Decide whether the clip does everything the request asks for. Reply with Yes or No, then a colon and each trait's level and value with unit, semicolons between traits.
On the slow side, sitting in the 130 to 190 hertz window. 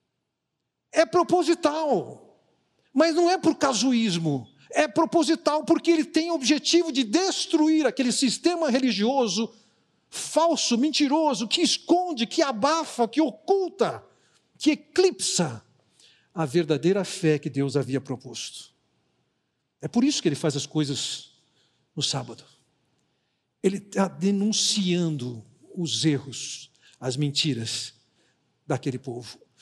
No: slow, 110 wpm; high, 210 Hz